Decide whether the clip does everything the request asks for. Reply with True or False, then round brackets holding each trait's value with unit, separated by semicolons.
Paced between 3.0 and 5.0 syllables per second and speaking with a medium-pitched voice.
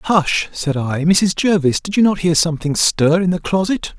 True (4.6 syllables/s; 175 Hz)